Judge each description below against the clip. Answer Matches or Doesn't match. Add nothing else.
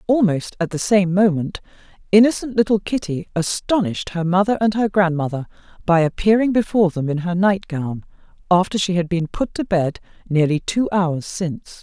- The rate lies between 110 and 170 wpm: Matches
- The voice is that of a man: Doesn't match